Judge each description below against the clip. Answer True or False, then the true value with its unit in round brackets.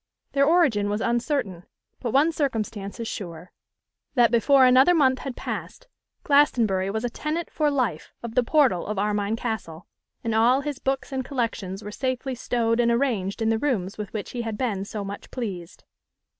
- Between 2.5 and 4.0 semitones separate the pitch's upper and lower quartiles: False (4.5 semitones)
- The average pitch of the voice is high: True (235 Hz)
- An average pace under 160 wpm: False (180 wpm)